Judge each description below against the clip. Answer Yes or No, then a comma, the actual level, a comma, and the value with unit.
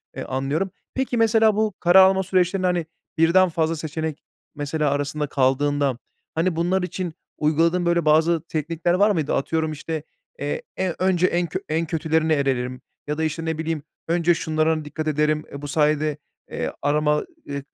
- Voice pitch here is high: No, medium, 160 Hz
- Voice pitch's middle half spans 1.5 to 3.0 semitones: Yes, average, 2.7 semitones